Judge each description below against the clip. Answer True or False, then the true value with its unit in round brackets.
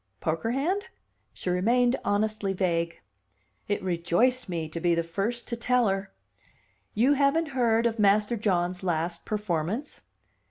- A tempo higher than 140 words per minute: False (135 wpm)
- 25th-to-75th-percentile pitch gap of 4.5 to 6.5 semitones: True (5.5 semitones)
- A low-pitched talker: False (205 Hz)